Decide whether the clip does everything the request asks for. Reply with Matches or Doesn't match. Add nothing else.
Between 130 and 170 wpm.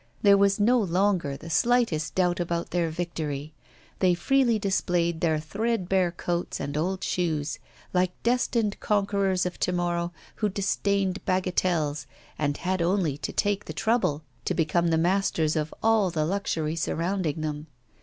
Matches